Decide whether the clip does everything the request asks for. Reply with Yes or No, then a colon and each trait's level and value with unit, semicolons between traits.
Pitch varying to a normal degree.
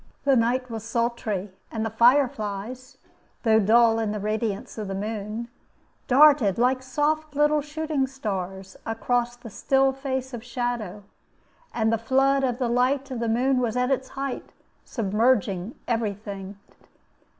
Yes: average, 3.5 semitones